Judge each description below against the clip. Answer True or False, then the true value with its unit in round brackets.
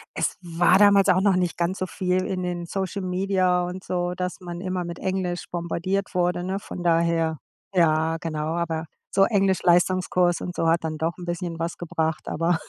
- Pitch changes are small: True (1.7 semitones)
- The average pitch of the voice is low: False (175 Hz)